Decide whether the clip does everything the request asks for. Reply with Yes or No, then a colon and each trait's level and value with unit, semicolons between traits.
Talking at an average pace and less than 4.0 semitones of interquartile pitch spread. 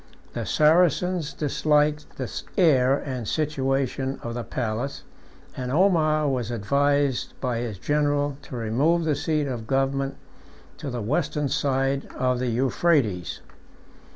No: slow, 125 wpm; average, 3.2 semitones